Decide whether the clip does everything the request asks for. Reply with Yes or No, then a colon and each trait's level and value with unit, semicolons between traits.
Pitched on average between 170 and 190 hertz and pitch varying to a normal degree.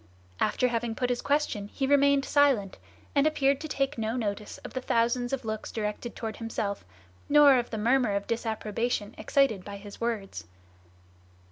No: high, 235 Hz; average, 4.2 semitones